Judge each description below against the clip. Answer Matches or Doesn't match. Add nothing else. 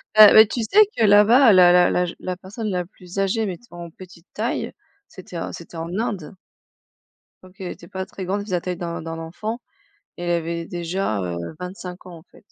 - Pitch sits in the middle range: Matches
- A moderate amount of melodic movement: Matches